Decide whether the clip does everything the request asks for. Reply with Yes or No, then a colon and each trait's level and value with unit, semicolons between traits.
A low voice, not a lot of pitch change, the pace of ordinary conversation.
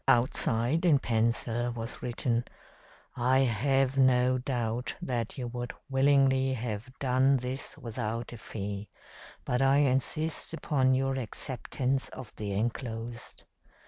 No: low, 125 Hz; narrow, 2.3 semitones; slow, 120 wpm